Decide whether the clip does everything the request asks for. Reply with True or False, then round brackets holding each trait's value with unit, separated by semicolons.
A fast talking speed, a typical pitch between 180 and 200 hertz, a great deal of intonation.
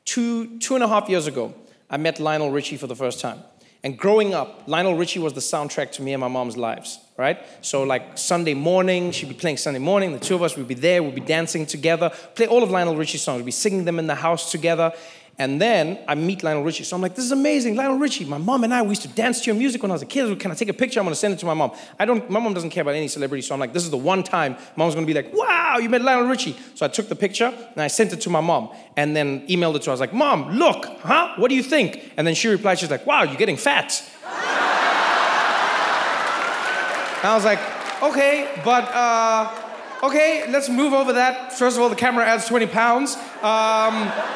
True (260 wpm; 190 Hz; 7.0 semitones)